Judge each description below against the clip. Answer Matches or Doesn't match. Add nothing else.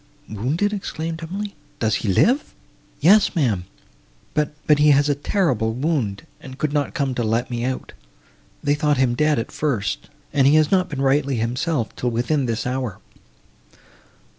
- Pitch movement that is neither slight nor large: Matches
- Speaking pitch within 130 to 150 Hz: Matches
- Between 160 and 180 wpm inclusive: Matches